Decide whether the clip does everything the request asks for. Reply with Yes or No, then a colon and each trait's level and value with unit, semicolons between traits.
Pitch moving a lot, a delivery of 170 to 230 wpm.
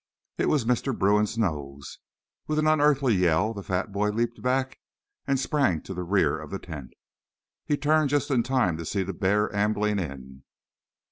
Yes: wide, 6.5 semitones; average, 180 wpm